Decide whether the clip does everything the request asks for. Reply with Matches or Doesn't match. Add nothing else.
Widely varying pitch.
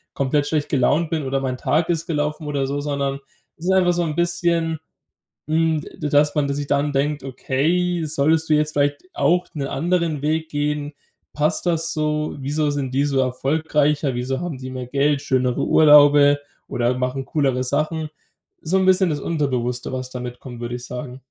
Doesn't match